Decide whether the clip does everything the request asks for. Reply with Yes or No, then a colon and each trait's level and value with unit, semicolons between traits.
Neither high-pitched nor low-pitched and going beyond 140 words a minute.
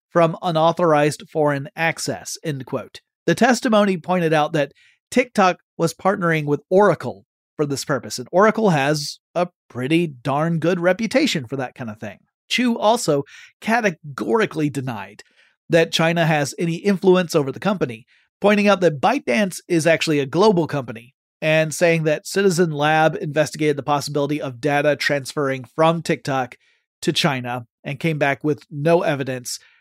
Yes: medium, 155 Hz; average, 150 wpm